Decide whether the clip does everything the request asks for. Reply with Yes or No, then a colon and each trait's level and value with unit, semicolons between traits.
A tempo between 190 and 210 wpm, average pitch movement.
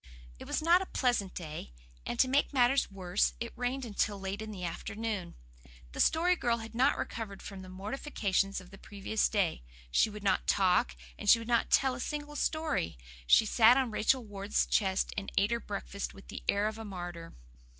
Yes: average, 200 wpm; average, 4.0 semitones